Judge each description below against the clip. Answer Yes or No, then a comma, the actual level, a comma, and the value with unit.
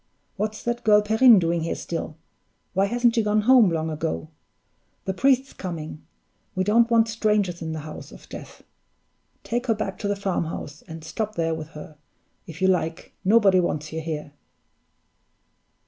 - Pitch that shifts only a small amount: No, average, 5.2 semitones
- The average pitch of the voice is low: No, high, 190 Hz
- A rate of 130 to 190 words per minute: Yes, average, 165 wpm